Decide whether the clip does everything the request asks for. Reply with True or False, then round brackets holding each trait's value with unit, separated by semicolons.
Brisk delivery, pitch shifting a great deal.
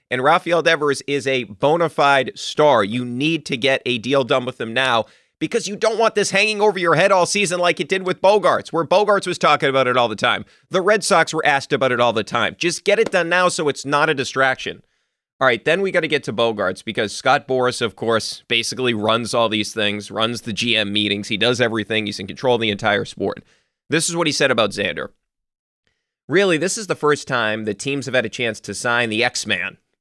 True (240 wpm; 6.6 semitones)